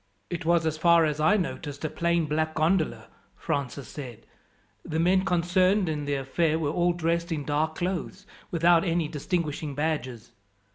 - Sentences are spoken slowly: No, average, 160 wpm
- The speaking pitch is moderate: Yes, medium, 160 Hz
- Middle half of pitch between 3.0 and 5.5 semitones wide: No, narrow, 2.5 semitones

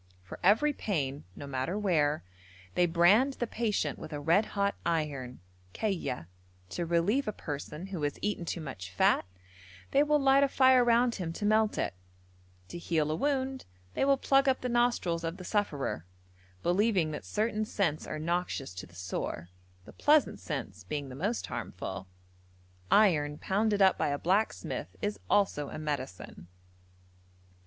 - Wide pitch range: Yes, wide, 6.9 semitones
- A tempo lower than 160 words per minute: No, average, 165 wpm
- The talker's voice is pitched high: No, medium, 180 Hz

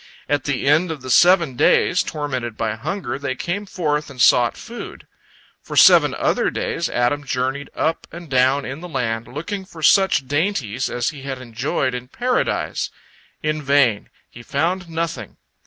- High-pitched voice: No, medium, 140 Hz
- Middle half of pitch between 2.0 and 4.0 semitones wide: No, average, 4.4 semitones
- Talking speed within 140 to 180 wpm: Yes, average, 165 wpm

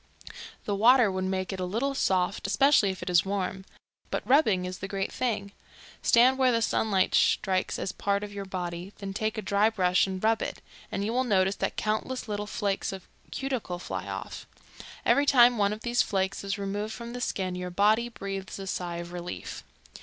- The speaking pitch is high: Yes, high, 200 Hz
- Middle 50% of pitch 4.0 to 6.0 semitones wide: No, average, 3.0 semitones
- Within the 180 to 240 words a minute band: Yes, average, 200 wpm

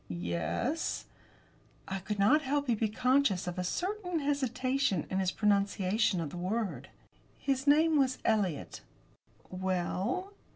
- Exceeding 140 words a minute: No, slow, 135 wpm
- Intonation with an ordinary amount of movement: No, wide, 7.3 semitones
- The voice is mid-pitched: No, high, 215 Hz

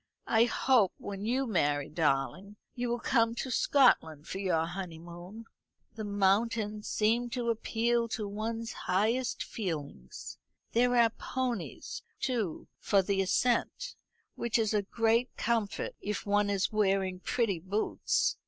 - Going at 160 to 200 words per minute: No, slow, 135 wpm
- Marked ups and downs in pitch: No, average, 3.6 semitones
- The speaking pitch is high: Yes, high, 210 Hz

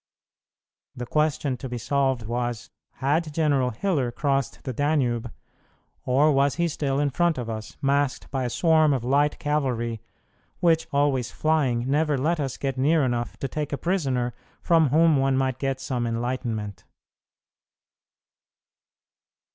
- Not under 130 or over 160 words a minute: Yes, average, 145 wpm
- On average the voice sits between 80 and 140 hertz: Yes, low, 135 Hz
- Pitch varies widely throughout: No, average, 3.5 semitones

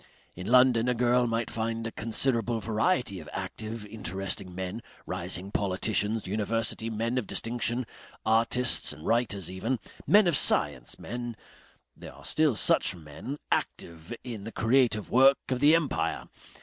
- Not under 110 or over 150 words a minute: Yes, average, 145 wpm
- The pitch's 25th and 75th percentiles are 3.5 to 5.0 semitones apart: Yes, average, 3.8 semitones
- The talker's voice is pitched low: Yes, low, 115 Hz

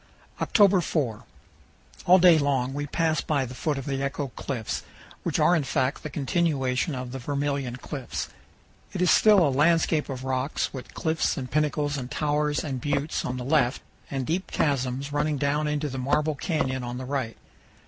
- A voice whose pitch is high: No, medium, 140 Hz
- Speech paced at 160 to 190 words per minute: Yes, average, 180 wpm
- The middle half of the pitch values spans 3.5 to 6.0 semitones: No, average, 2.7 semitones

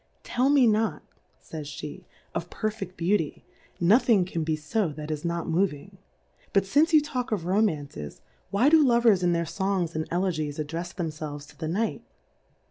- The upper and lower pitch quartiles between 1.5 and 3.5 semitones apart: No, wide, 5.5 semitones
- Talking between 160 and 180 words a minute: Yes, average, 170 wpm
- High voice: No, medium, 180 Hz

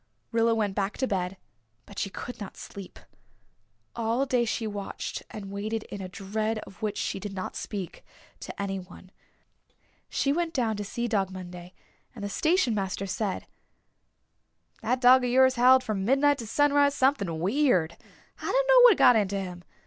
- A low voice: No, high, 215 Hz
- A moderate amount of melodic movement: Yes, average, 4.9 semitones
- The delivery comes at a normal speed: Yes, average, 170 wpm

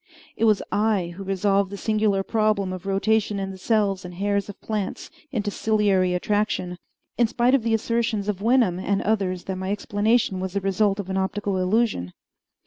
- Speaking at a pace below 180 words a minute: No, average, 185 wpm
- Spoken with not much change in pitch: Yes, narrow, 2.3 semitones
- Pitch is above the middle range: Yes, high, 200 Hz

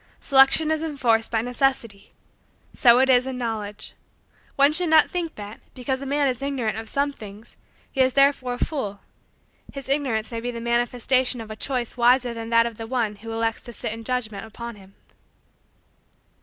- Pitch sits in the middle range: No, high, 245 Hz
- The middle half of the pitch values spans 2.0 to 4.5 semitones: Yes, average, 3.1 semitones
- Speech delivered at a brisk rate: No, average, 185 wpm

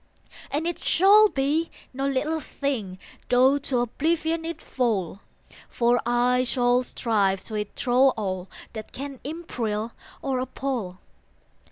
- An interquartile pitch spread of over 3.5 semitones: Yes, average, 4.1 semitones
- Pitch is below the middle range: No, very high, 255 Hz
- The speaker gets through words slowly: Yes, slow, 130 wpm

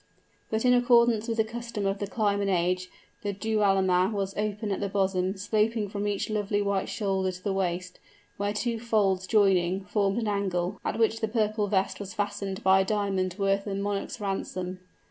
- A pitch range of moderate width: No, narrow, 2.0 semitones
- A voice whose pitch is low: No, high, 200 Hz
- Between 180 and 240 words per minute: Yes, average, 195 wpm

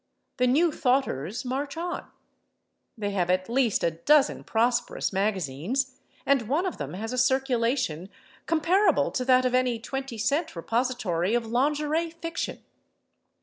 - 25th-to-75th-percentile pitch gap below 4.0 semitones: No, average, 4.5 semitones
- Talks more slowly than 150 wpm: Yes, average, 140 wpm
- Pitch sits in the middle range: No, very high, 250 Hz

